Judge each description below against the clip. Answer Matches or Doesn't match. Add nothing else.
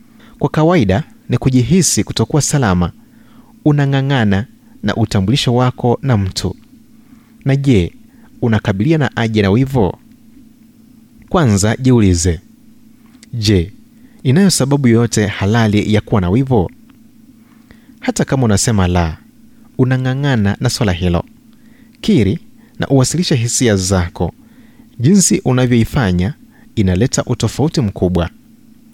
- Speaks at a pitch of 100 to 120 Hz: Doesn't match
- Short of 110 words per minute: Matches